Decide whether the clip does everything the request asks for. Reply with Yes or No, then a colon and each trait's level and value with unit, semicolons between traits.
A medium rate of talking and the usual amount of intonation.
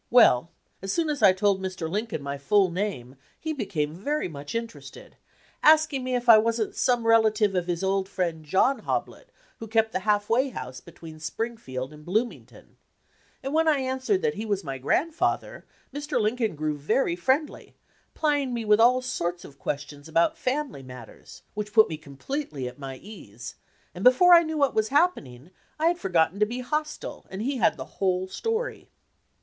No: average, 190 wpm; wide, 8.1 semitones